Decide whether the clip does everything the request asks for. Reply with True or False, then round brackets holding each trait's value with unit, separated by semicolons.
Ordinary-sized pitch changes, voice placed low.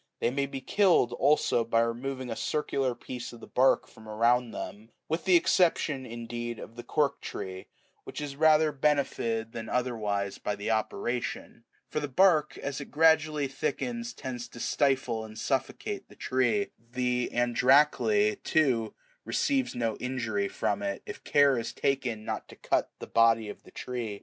True (4.2 semitones; 125 Hz)